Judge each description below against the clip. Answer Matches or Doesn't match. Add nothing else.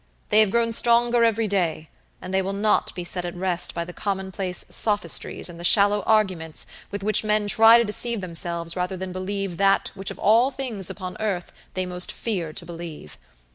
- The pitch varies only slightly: Doesn't match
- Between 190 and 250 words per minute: Matches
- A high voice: Matches